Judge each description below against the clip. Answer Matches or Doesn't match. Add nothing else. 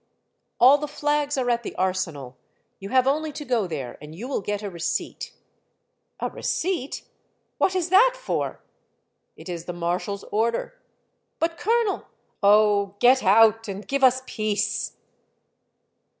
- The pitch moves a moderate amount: Doesn't match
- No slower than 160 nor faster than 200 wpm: Matches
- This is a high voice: Matches